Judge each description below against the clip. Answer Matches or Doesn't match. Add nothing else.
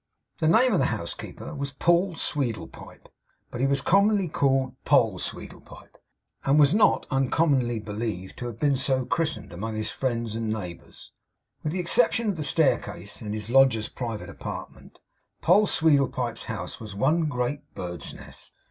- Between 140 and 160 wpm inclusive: Matches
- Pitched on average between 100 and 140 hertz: Matches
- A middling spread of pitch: Doesn't match